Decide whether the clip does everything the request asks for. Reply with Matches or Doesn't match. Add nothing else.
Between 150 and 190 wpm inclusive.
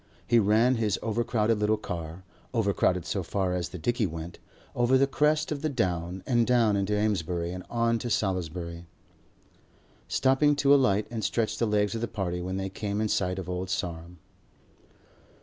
Matches